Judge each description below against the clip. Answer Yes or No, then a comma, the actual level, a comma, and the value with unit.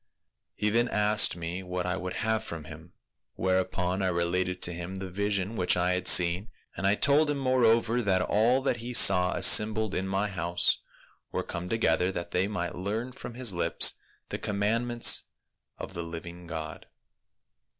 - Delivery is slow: No, average, 175 wpm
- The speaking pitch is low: Yes, very low, 95 Hz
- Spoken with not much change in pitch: No, average, 3.8 semitones